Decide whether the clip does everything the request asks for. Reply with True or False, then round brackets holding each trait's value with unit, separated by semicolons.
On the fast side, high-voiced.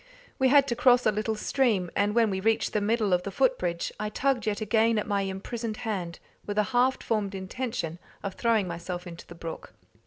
True (215 wpm; 210 Hz)